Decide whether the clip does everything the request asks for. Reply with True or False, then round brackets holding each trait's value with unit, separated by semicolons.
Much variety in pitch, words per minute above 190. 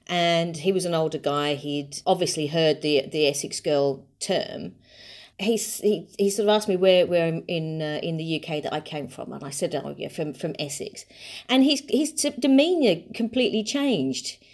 True (6.0 semitones; 200 wpm)